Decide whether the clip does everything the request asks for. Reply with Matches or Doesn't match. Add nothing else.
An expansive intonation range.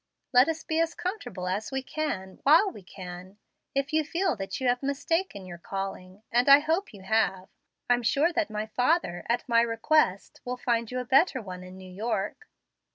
Matches